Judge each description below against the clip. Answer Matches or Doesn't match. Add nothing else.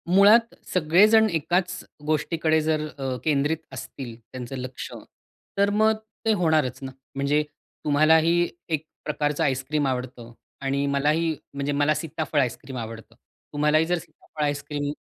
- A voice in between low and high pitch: Matches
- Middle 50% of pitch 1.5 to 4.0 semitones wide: Matches